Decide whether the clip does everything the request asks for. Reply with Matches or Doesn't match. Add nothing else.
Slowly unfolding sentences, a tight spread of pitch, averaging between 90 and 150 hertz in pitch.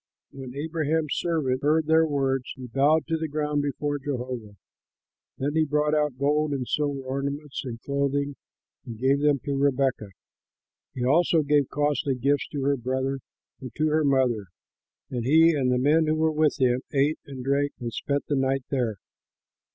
Doesn't match